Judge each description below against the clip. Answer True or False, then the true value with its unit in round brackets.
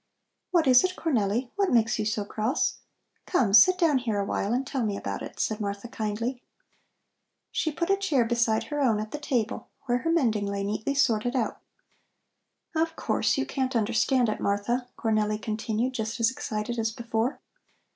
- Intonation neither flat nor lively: True (3.8 semitones)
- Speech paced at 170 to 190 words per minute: True (180 wpm)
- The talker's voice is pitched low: False (235 Hz)